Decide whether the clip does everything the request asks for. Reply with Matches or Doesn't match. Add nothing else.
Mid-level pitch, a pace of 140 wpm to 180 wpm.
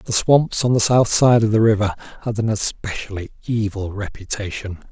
Doesn't match